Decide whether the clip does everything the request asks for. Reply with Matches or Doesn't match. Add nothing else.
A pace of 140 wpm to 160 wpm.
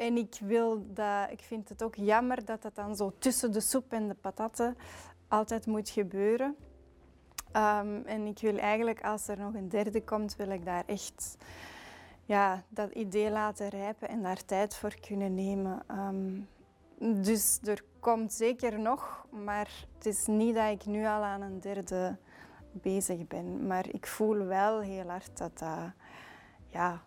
Doesn't match